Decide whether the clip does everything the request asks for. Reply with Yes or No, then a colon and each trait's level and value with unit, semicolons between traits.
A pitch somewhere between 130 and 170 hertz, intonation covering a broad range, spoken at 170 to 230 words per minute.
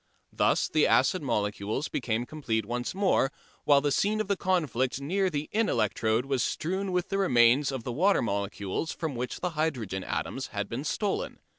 Yes: medium, 140 Hz; wide, 7.4 semitones; average, 180 wpm